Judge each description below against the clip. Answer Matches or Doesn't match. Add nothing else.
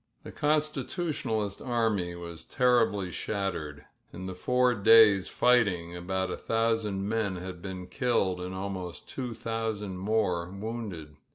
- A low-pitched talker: Matches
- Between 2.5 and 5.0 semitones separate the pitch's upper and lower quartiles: Matches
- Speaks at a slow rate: Matches